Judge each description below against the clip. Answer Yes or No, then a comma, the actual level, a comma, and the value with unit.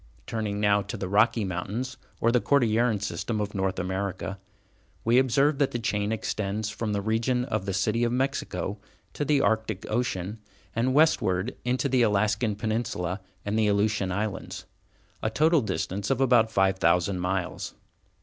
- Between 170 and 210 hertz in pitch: No, low, 105 Hz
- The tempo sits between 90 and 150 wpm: No, average, 160 wpm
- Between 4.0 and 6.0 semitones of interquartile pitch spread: No, average, 3.6 semitones